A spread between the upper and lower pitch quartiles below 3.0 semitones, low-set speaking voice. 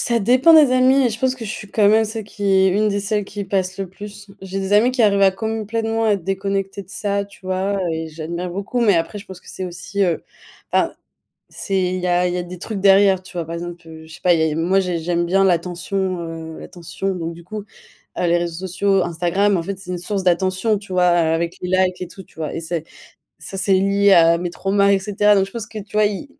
No: narrow, 2.6 semitones; high, 190 Hz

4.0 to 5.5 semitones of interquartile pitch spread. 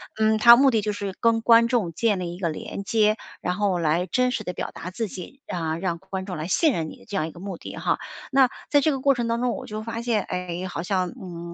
Yes: average, 4.6 semitones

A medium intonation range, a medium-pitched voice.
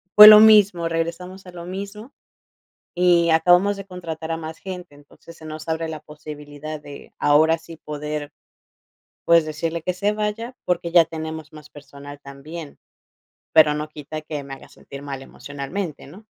Yes: average, 3.1 semitones; medium, 160 Hz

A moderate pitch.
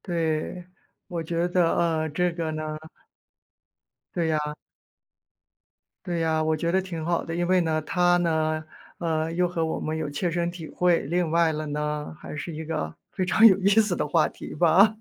Yes: medium, 165 Hz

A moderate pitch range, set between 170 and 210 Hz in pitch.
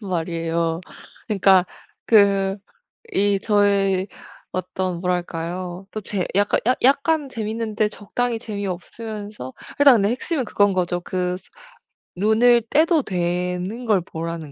Yes: average, 3.5 semitones; high, 200 Hz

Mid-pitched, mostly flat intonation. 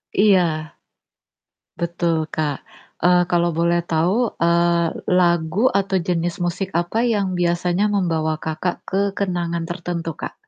Yes: medium, 175 Hz; narrow, 1.3 semitones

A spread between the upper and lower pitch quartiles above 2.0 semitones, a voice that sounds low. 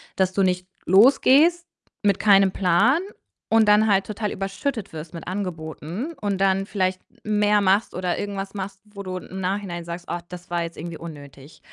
No: narrow, 2.6 semitones; high, 195 Hz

